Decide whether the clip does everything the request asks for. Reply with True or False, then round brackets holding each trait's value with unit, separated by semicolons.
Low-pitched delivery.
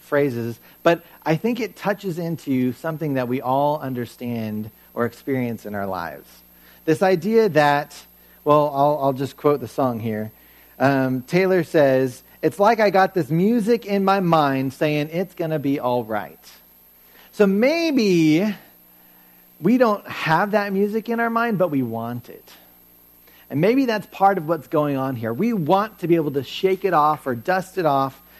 False (145 Hz)